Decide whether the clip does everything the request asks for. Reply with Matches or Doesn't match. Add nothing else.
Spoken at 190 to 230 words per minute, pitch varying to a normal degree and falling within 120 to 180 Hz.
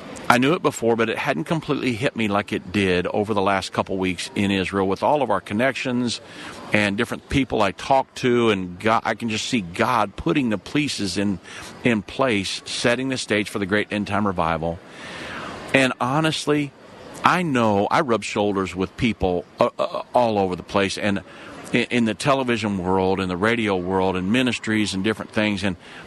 Doesn't match